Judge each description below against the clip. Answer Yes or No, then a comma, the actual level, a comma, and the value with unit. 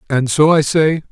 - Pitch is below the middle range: No, medium, 150 Hz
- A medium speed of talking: No, fast, 215 wpm